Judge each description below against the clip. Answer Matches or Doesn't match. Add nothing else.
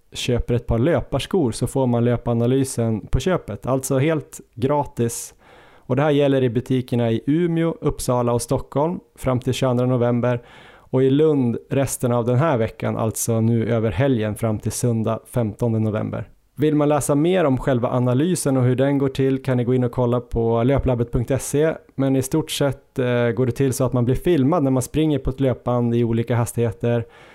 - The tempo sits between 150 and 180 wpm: Doesn't match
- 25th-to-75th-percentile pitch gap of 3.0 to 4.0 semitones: Doesn't match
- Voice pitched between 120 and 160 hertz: Matches